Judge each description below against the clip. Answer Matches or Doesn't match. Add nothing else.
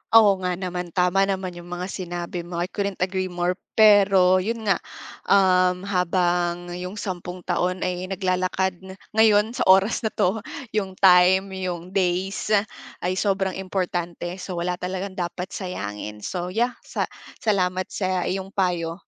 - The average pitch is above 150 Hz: Matches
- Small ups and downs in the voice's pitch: Matches